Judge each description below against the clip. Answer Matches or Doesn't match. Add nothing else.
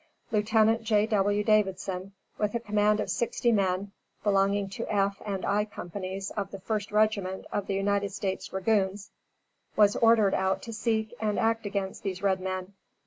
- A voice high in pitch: Matches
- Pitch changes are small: Matches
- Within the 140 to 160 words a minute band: Matches